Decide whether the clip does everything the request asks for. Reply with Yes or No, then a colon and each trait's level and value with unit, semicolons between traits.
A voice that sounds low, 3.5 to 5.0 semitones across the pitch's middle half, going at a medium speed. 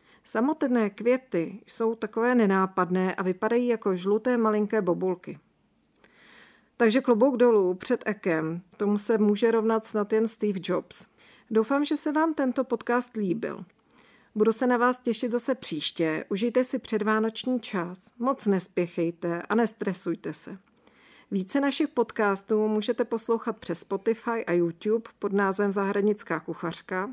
No: high, 220 Hz; average, 3.8 semitones; average, 135 wpm